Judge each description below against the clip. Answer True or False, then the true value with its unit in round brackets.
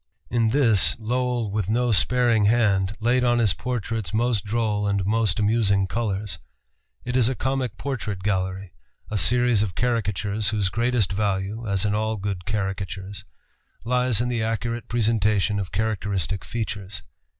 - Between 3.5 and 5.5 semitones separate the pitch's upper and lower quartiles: False (3.0 semitones)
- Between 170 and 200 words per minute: False (145 wpm)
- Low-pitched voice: True (110 Hz)